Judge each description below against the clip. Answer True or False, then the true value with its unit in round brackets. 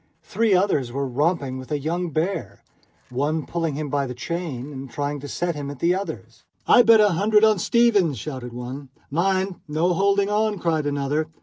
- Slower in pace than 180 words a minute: False (190 wpm)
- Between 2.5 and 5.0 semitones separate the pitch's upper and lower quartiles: False (5.4 semitones)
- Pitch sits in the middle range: True (160 Hz)